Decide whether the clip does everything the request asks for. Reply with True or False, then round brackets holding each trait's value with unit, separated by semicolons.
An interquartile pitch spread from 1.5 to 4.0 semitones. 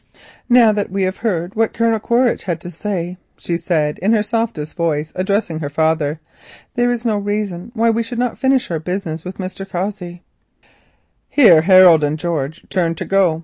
False (4.8 semitones)